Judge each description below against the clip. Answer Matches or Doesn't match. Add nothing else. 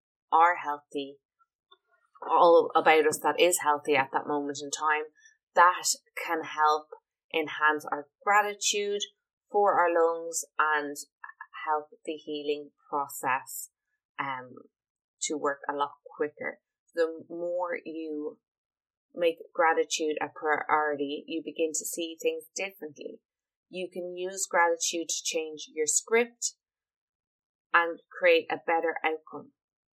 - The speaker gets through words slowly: Matches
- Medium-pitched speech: Matches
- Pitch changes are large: Matches